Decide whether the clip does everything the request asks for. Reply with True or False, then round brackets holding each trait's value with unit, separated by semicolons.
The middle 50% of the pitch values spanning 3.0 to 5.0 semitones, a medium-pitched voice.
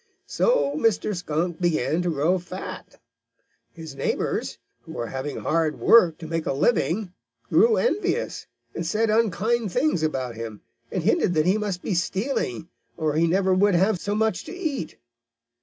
False (5.4 semitones; 180 Hz)